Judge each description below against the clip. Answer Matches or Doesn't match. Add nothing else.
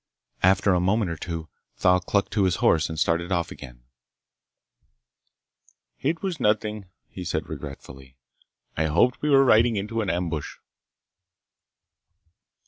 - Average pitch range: Matches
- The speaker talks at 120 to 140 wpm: Matches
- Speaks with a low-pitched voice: Matches